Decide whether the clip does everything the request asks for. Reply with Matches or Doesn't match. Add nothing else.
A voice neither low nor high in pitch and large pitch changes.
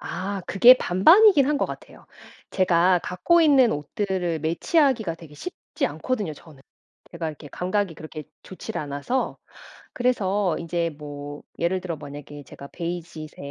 Doesn't match